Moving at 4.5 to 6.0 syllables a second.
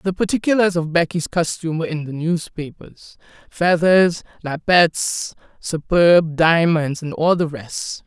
No: 4.2 syllables/s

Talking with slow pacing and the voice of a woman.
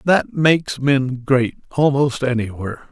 No: slow, 125 wpm; male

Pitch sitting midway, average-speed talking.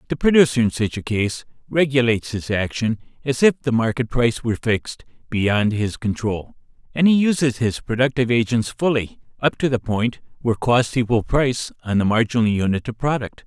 No: low, 120 Hz; average, 180 wpm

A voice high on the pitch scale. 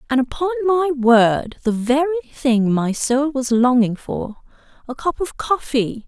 Yes: very high, 270 Hz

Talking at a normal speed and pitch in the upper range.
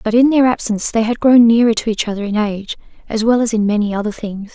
No: fast, 265 wpm; high, 220 Hz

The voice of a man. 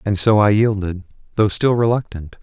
Yes: male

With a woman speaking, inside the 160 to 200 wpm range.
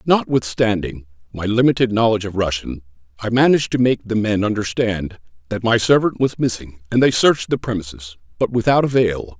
No: male; average, 165 wpm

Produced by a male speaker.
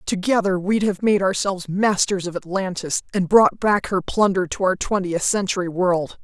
No: female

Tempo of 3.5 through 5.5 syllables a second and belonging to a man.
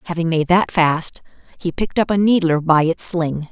No: 5.0 syllables/s; female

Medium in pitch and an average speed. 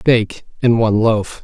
No: low, 110 Hz; average, 170 wpm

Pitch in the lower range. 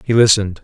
Yes: low, 105 Hz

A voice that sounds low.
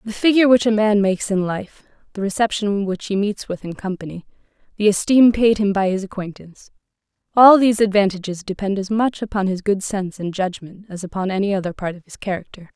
No: high, 200 Hz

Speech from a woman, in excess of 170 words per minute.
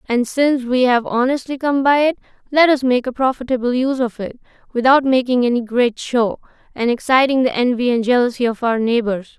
Yes: female; average, 190 wpm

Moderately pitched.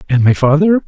Yes: medium, 155 Hz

